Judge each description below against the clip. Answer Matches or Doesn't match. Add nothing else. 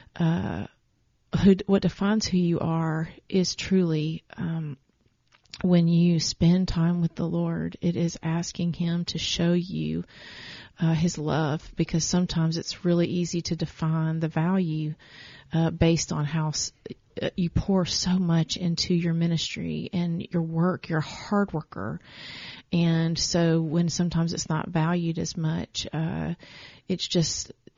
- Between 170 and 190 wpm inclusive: Doesn't match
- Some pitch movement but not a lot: Doesn't match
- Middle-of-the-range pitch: Matches